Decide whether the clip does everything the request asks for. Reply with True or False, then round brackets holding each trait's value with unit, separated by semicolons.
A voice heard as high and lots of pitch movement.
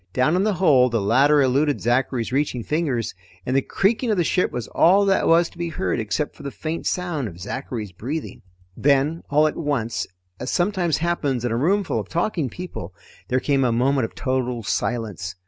False (140 Hz; 5.7 semitones)